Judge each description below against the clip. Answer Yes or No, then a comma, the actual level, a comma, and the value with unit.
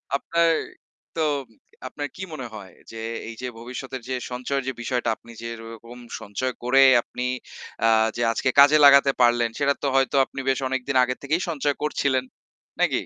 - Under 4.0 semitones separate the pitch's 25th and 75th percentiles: Yes, average, 2.8 semitones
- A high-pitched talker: No, low, 130 Hz